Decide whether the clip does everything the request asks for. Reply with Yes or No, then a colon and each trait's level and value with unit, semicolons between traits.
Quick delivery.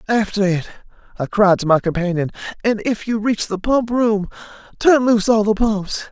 No: average, 185 wpm